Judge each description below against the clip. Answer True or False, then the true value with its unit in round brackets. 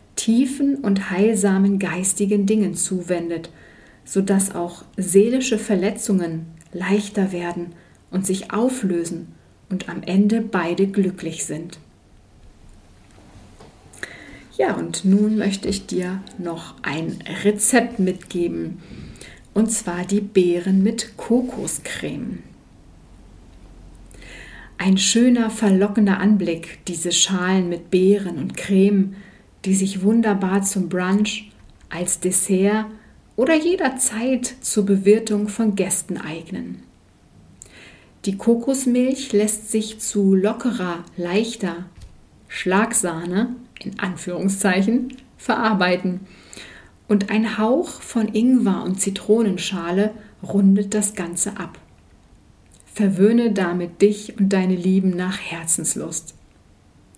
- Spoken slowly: True (95 wpm)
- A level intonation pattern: False (3.3 semitones)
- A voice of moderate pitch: False (195 Hz)